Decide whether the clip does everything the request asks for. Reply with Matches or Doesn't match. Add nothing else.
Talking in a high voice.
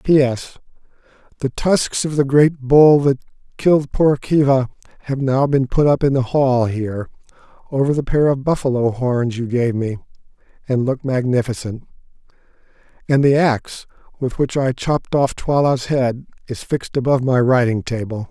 Doesn't match